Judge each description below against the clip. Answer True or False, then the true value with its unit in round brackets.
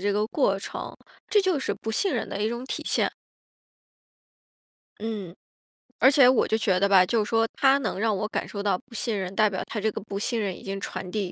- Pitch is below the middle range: False (215 Hz)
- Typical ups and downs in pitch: True (3.1 semitones)